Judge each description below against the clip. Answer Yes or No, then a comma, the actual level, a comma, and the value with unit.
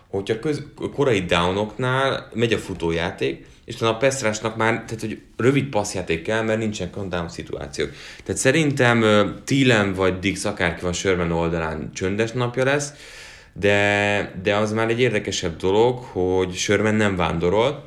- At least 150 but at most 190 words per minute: Yes, fast, 155 wpm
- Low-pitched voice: Yes, low, 105 Hz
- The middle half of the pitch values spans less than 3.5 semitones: No, average, 3.9 semitones